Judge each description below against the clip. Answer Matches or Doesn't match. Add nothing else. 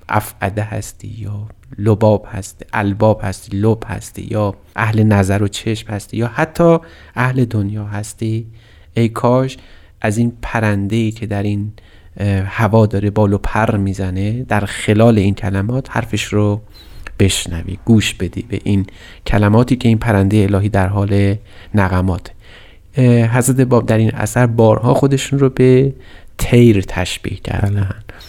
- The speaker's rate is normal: Matches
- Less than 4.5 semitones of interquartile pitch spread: Matches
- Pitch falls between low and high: Doesn't match